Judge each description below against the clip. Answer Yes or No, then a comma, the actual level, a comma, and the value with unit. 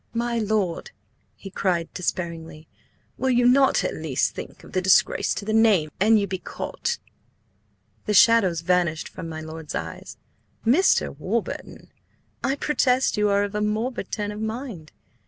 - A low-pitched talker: No, high, 205 Hz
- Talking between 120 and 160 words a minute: Yes, average, 155 wpm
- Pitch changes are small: No, average, 5.1 semitones